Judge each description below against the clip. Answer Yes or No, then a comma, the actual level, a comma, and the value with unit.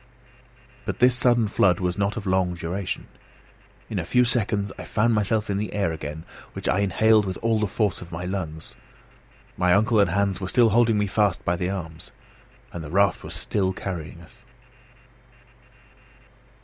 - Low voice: Yes, low, 100 Hz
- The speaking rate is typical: Yes, average, 175 wpm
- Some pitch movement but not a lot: Yes, average, 3.3 semitones